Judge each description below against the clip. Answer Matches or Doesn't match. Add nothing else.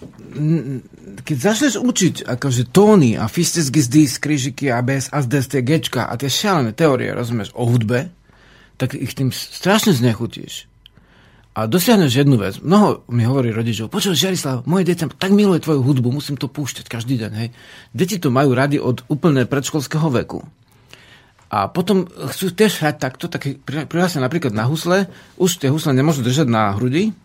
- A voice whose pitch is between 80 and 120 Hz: Doesn't match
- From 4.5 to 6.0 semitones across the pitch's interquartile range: Matches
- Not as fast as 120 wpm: Doesn't match